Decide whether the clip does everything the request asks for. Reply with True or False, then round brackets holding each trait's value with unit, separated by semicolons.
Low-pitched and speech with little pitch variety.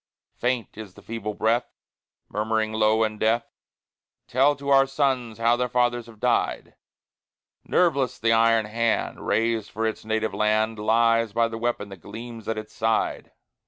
True (115 Hz; 1.6 semitones)